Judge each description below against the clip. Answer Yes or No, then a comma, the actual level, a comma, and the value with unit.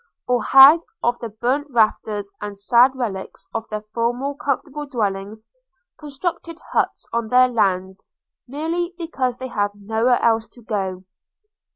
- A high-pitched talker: Yes, high, 235 Hz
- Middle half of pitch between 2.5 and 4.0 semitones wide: No, average, 4.4 semitones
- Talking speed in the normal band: Yes, average, 145 wpm